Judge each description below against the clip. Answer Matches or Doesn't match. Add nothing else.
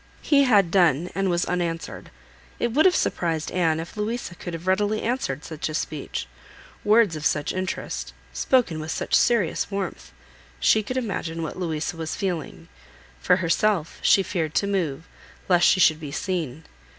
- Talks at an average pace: Matches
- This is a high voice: Doesn't match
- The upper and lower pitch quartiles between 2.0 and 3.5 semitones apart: Doesn't match